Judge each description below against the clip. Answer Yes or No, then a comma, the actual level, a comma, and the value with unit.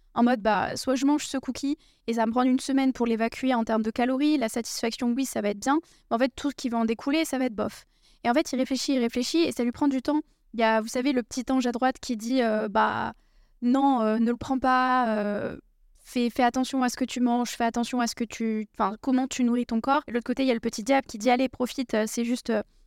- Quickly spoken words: Yes, fast, 290 wpm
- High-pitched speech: Yes, very high, 250 Hz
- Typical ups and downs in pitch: No, narrow, 2.3 semitones